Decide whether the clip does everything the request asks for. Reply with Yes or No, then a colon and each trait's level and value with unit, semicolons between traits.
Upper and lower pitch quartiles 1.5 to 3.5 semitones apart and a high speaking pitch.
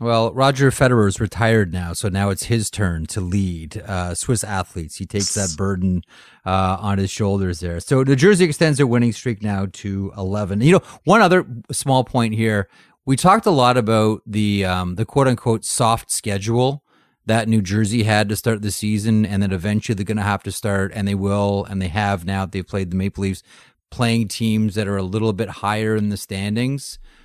No: average, 3.1 semitones; low, 105 Hz